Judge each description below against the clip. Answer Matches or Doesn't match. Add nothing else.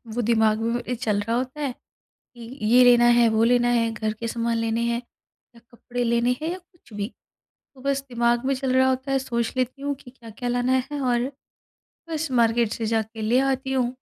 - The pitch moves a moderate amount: Doesn't match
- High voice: Matches